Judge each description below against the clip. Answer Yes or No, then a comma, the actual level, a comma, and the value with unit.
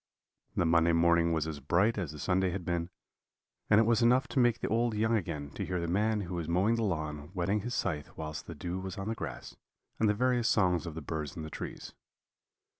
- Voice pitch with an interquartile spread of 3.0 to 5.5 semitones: Yes, average, 4.9 semitones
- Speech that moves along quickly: Yes, fast, 235 wpm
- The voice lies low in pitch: Yes, very low, 90 Hz